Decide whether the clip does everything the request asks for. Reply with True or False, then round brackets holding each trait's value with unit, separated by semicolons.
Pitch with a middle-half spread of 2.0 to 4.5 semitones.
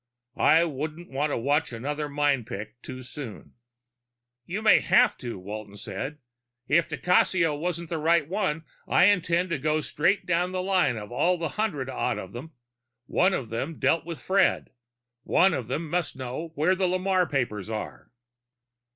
False (5.4 semitones)